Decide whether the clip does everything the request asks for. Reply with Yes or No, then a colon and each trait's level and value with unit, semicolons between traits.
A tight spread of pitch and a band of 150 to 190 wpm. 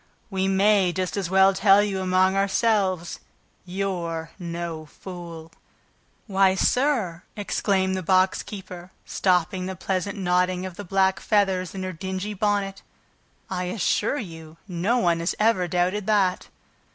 No: narrow, 1.8 semitones; average, 140 wpm